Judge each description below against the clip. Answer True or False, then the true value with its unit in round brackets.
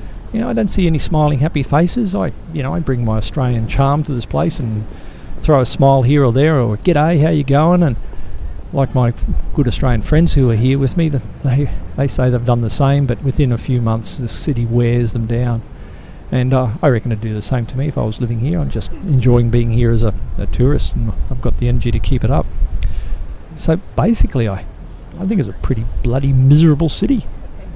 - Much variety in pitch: False (4.3 semitones)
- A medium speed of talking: False (230 wpm)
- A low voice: True (125 Hz)